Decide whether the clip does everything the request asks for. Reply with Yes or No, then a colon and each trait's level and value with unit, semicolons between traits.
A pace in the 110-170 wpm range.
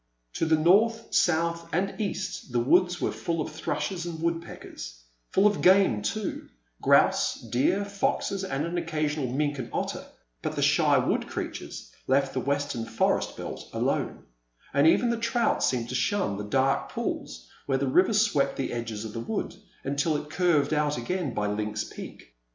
No: average, 180 wpm